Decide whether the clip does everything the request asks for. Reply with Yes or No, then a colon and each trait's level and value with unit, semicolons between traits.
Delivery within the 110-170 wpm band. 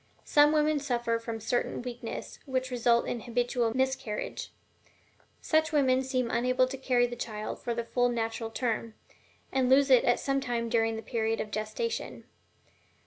Yes: average, 160 wpm